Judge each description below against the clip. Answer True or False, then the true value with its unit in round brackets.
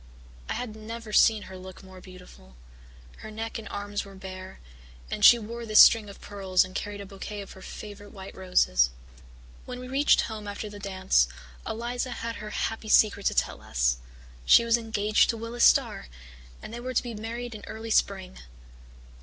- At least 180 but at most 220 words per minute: True (185 wpm)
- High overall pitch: True (210 Hz)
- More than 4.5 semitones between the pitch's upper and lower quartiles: False (3.1 semitones)